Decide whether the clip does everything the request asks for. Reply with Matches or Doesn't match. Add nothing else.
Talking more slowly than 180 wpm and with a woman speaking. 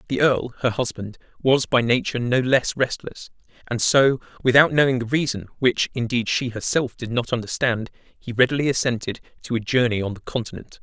Doesn't match